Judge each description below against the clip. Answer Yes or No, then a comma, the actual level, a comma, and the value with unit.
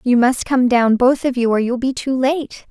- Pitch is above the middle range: Yes, very high, 250 Hz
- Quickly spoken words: Yes, fast, 265 wpm